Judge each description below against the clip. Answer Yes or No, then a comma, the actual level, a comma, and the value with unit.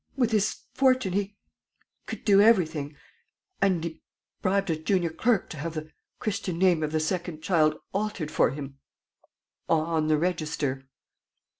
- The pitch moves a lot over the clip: No, average, 4.2 semitones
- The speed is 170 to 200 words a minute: No, average, 145 wpm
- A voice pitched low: No, medium, 170 Hz